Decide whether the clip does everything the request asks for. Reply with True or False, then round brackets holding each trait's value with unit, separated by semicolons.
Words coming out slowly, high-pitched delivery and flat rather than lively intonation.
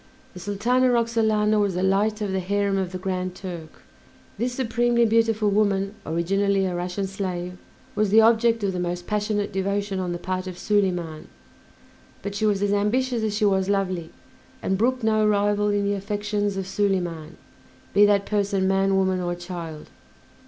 False (175 wpm; 200 Hz; 2.2 semitones)